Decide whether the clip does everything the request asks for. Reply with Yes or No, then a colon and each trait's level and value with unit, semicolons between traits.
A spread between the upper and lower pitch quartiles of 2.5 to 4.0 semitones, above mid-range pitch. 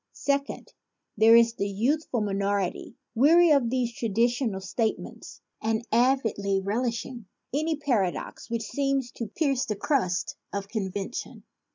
No: average, 4.8 semitones; high, 230 Hz